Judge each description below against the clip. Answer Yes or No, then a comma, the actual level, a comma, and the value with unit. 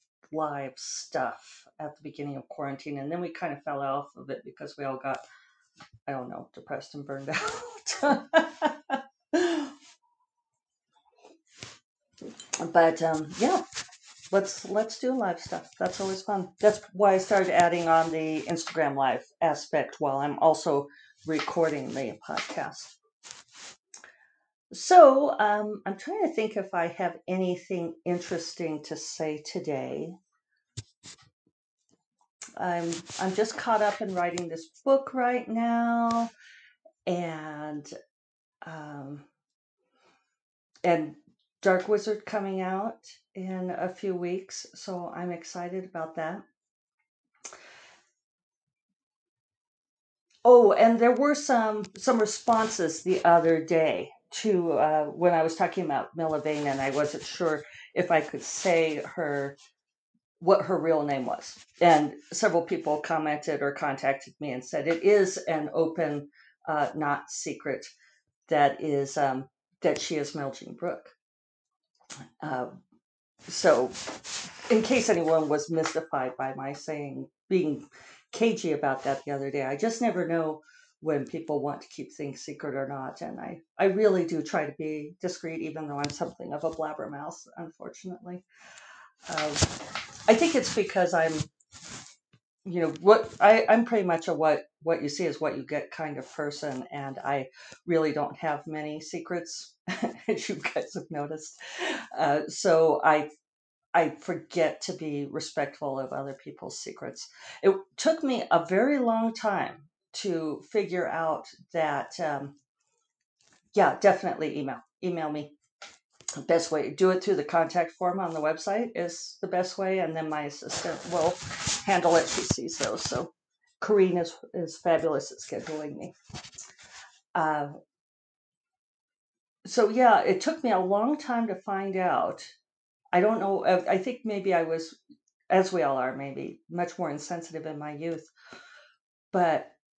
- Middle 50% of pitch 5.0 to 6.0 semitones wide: Yes, wide, 5.6 semitones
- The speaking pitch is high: No, medium, 170 Hz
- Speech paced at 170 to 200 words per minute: No, average, 140 wpm